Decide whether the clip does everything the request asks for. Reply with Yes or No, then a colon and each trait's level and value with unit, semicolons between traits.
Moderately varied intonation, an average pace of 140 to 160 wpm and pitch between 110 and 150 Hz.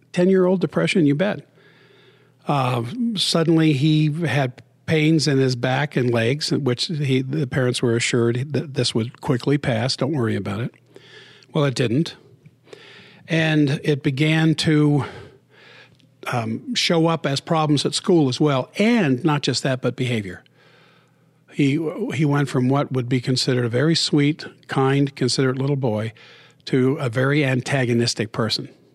Yes: average, 3.4 semitones; average, 150 wpm; medium, 140 Hz